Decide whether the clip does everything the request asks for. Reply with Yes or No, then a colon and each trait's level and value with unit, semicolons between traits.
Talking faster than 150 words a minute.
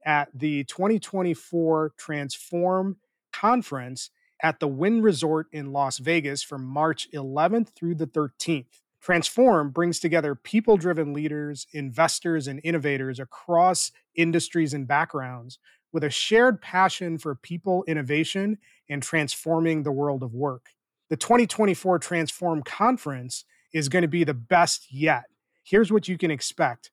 No: slow, 135 wpm